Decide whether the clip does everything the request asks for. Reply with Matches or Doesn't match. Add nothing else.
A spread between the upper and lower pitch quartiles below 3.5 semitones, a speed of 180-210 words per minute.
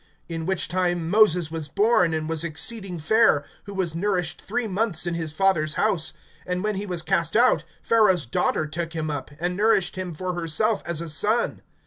Doesn't match